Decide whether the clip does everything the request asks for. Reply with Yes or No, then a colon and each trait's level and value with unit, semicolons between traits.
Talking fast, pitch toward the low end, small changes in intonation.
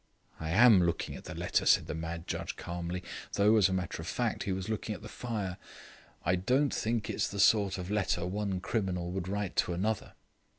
No: fast, 210 wpm; very low, 95 Hz; average, 3.2 semitones